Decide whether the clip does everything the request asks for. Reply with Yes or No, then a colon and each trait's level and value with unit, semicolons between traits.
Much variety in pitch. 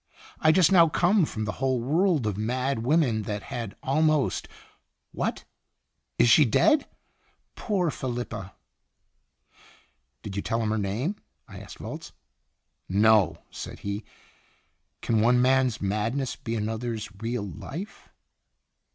Yes: wide, 5.7 semitones